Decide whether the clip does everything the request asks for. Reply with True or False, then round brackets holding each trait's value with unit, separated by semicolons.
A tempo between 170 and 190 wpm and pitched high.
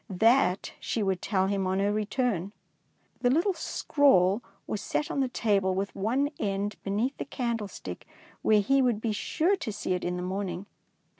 True (180 wpm; 210 Hz)